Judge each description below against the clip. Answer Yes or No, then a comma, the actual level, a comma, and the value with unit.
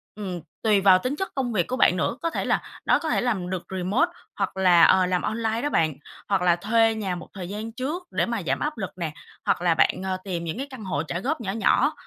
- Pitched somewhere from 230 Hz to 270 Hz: No, high, 195 Hz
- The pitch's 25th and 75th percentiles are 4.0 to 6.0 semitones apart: Yes, average, 4.5 semitones